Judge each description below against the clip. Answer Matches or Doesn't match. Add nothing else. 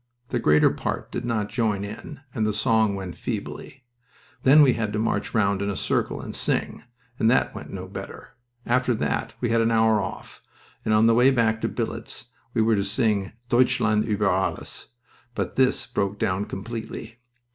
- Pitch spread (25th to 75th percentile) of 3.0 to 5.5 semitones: Doesn't match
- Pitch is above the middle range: Doesn't match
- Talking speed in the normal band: Matches